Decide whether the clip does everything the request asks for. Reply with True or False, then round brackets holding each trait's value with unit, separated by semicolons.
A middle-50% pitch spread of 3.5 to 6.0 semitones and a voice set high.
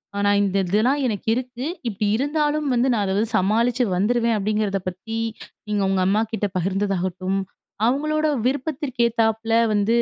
True (3.8 semitones; 225 Hz)